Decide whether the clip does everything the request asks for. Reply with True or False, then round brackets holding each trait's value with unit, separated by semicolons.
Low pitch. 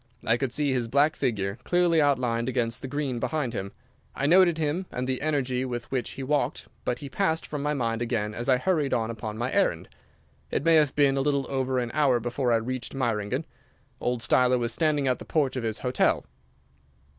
True (130 Hz)